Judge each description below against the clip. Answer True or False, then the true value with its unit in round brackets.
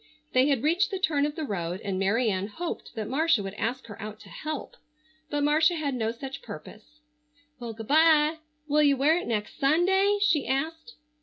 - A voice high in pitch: True (285 Hz)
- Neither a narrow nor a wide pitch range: False (6.1 semitones)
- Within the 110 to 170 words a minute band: False (200 wpm)